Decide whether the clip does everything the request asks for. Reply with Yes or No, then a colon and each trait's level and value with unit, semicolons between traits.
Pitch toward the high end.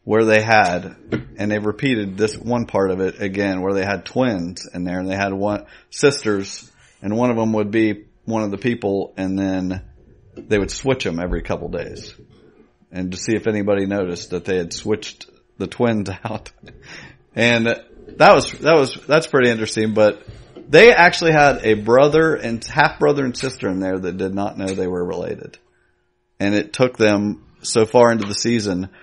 No: low, 105 Hz